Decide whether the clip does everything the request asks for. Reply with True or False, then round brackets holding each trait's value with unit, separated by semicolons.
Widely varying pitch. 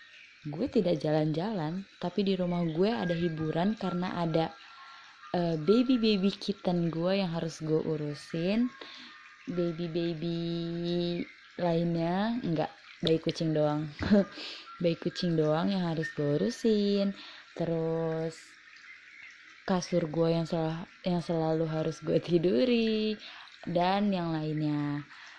False (3.1 semitones)